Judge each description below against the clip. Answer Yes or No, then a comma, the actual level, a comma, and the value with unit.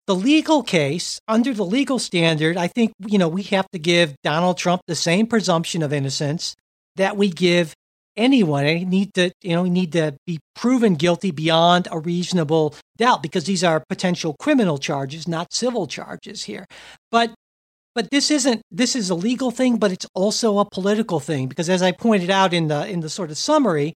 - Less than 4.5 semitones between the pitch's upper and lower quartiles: No, average, 4.9 semitones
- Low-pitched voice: No, medium, 185 Hz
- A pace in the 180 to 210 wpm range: Yes, average, 200 wpm